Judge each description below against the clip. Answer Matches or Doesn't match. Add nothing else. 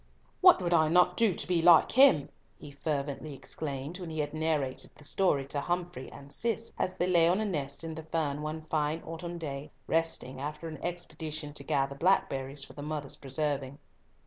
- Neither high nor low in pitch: Matches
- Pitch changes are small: Doesn't match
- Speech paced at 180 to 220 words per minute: Matches